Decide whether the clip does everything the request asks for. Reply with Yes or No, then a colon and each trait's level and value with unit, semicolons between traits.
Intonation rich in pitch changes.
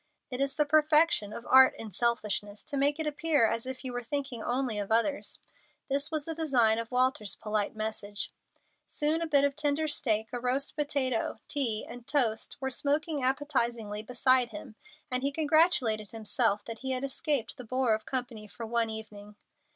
No: average, 4.5 semitones